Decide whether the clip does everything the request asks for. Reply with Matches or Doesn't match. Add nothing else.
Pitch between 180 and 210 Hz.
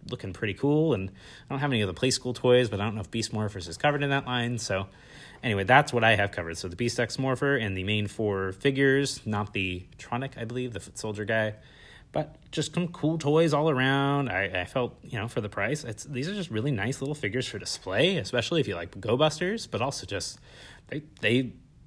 Doesn't match